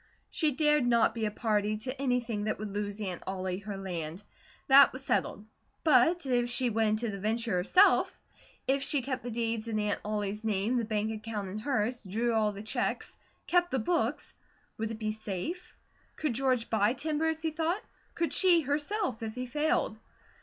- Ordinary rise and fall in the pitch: Yes, average, 4.5 semitones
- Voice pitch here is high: Yes, high, 230 Hz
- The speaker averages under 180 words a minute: No, average, 190 wpm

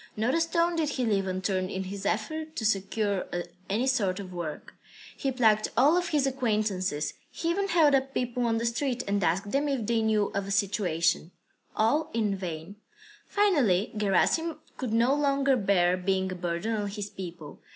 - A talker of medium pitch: No, high, 215 Hz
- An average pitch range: No, wide, 5.9 semitones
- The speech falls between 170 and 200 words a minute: Yes, average, 185 wpm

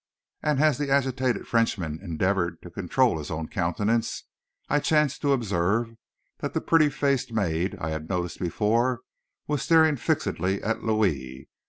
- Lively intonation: Yes, wide, 7.5 semitones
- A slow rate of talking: No, average, 150 wpm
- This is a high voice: No, low, 110 Hz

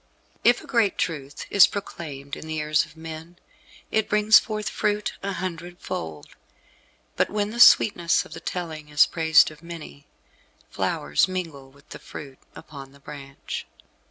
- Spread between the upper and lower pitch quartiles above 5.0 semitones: Yes, wide, 5.4 semitones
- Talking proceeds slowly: No, average, 155 wpm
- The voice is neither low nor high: Yes, medium, 160 Hz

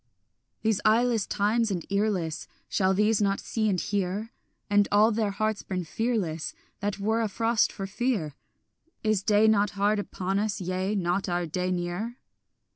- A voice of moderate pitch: No, high, 205 Hz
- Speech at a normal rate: Yes, average, 155 wpm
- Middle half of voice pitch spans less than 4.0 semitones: Yes, narrow, 2.6 semitones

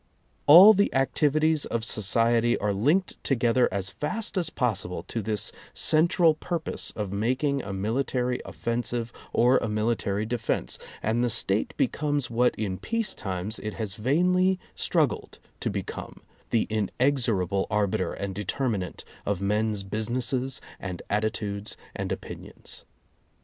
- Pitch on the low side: Yes, low, 115 Hz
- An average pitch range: Yes, average, 5.0 semitones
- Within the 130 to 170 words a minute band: Yes, slow, 135 wpm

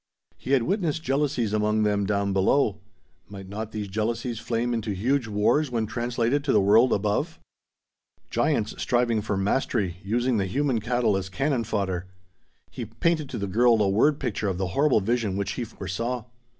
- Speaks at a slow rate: No, average, 175 wpm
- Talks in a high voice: No, low, 110 Hz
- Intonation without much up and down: No, average, 3.8 semitones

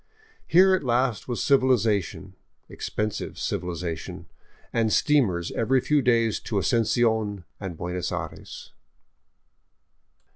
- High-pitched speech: No, low, 115 Hz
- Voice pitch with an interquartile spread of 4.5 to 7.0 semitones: Yes, average, 5.0 semitones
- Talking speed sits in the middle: No, slow, 110 wpm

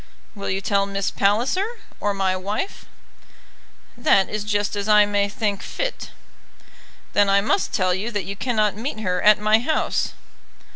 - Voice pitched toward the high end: Yes, high, 205 Hz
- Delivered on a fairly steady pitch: Yes, narrow, 1.7 semitones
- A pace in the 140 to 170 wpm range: Yes, average, 160 wpm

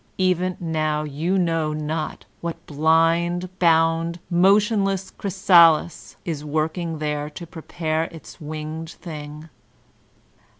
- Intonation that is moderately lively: No, narrow, 2.3 semitones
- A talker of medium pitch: Yes, medium, 165 Hz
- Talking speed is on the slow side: Yes, slow, 100 wpm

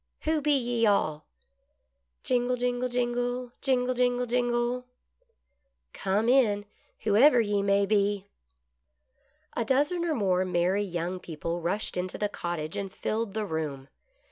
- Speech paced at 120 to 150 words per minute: Yes, average, 140 wpm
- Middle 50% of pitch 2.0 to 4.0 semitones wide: No, average, 5.0 semitones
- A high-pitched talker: Yes, high, 215 Hz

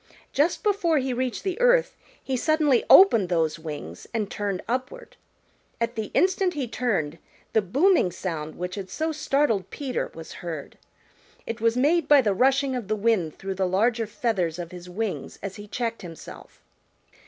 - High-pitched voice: Yes, high, 230 Hz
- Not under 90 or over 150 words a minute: No, average, 170 wpm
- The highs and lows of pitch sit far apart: Yes, wide, 7.3 semitones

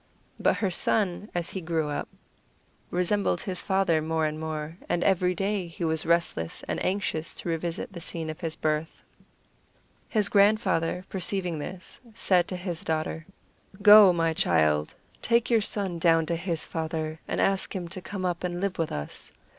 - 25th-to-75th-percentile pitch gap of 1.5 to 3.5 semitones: Yes, average, 3.1 semitones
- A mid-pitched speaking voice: Yes, medium, 175 Hz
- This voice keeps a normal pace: Yes, average, 170 wpm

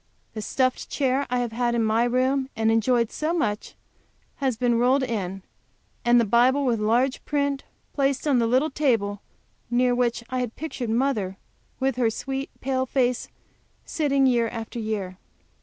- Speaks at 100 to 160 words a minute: No, average, 170 wpm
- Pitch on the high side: Yes, high, 245 Hz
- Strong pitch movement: No, average, 2.9 semitones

